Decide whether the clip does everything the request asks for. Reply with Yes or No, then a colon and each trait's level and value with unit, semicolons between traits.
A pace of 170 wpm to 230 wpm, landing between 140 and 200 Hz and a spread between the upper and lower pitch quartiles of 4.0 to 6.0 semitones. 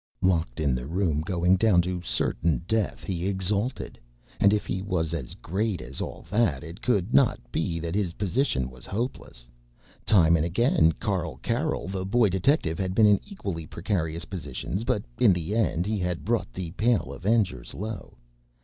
No: average, 175 wpm; very low, 95 Hz; average, 4.3 semitones